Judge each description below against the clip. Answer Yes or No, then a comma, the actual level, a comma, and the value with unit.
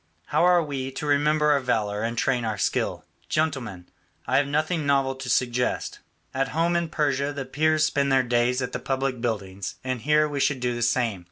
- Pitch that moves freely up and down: No, average, 3.5 semitones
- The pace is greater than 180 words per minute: Yes, average, 200 wpm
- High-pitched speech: No, low, 135 Hz